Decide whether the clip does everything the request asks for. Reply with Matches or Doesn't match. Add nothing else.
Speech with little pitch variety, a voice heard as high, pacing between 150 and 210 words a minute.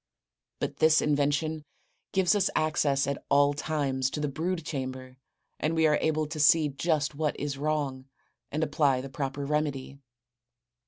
Doesn't match